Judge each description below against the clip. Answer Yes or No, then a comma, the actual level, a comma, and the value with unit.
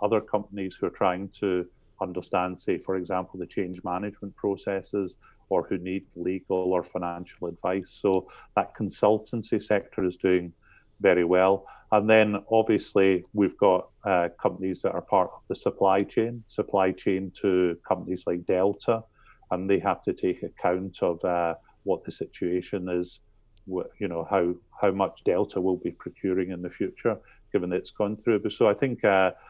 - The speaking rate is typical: Yes, average, 165 wpm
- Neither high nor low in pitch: No, very low, 95 Hz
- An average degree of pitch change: No, narrow, 2.0 semitones